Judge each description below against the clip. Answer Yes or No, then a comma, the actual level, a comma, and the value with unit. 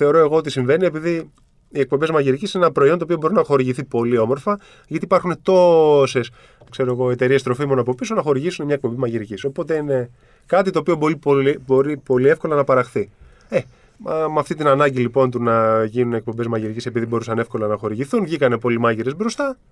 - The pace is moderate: No, fast, 190 wpm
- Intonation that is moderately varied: Yes, average, 4.9 semitones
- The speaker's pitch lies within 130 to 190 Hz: Yes, low, 135 Hz